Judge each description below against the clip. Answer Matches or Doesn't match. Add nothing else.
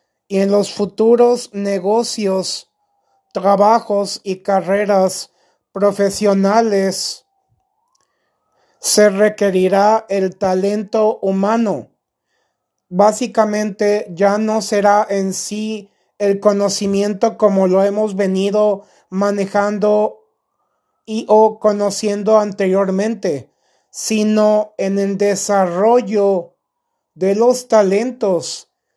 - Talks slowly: Matches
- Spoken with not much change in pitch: Matches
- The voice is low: Doesn't match